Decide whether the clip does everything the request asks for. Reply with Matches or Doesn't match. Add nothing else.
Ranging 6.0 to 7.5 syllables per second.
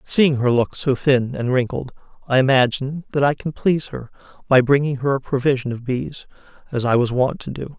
Doesn't match